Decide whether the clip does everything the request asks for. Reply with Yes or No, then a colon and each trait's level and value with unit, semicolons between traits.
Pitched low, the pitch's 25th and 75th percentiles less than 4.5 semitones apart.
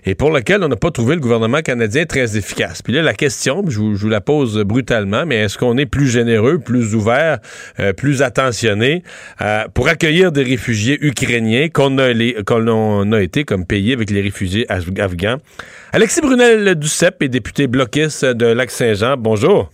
No: low, 125 Hz; average, 4.9 semitones